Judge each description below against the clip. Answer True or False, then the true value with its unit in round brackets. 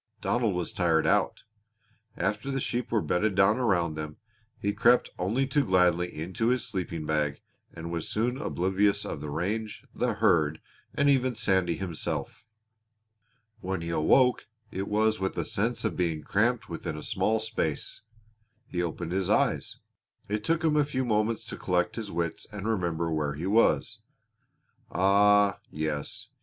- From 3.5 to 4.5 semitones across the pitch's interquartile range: False (4.9 semitones)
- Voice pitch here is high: False (95 Hz)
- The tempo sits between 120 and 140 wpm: False (160 wpm)